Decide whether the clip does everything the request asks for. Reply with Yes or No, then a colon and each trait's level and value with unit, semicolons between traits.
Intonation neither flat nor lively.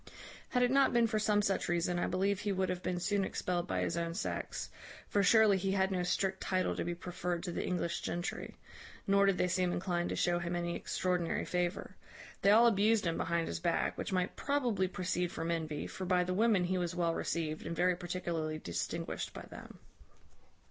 No: narrow, 2.3 semitones